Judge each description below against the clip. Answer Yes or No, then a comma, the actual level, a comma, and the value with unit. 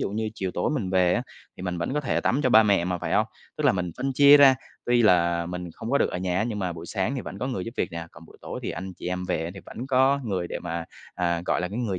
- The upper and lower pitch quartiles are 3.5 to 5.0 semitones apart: No, wide, 5.4 semitones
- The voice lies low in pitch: Yes, very low, 95 Hz